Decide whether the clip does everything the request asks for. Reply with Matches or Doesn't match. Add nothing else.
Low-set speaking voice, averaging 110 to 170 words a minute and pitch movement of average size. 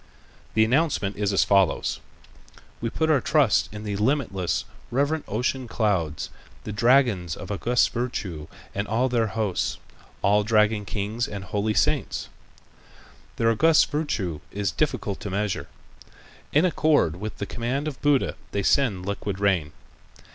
Matches